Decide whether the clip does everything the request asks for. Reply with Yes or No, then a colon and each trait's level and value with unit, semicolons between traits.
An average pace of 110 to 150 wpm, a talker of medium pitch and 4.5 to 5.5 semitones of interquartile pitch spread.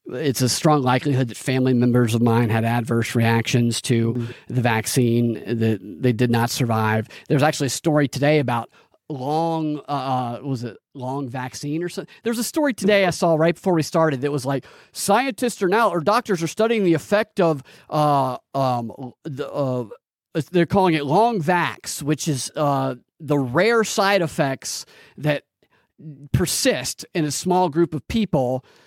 No: average, 170 wpm; medium, 145 Hz; average, 5.2 semitones